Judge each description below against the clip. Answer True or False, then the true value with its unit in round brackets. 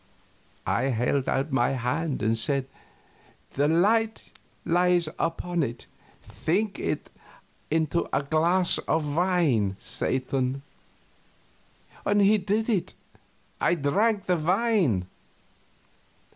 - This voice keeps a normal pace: False (100 wpm)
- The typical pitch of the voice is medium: True (160 Hz)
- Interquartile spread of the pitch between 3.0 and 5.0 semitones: False (5.5 semitones)